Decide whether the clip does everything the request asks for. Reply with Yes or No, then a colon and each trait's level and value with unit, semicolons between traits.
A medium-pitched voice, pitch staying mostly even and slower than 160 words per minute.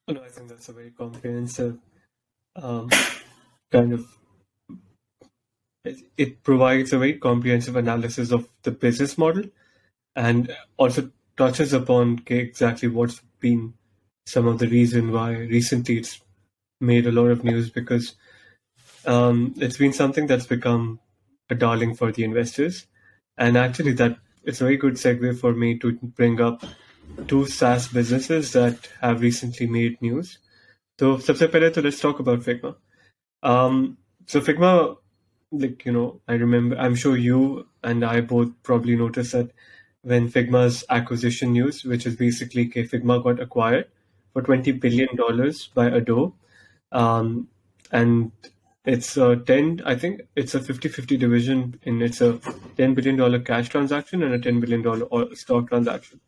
No: low, 120 Hz; narrow, 1.6 semitones; average, 150 wpm